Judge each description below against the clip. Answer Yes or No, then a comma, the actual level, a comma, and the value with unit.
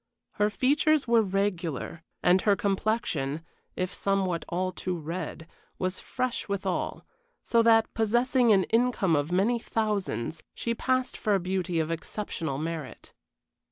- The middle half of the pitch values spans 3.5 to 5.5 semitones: Yes, average, 4.8 semitones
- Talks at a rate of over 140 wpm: No, slow, 135 wpm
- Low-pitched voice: No, high, 195 Hz